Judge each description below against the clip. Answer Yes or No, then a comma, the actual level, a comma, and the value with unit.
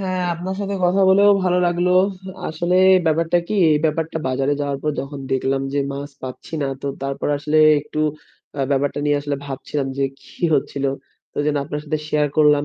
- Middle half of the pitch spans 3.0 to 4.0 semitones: Yes, average, 3.6 semitones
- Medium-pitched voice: Yes, medium, 150 Hz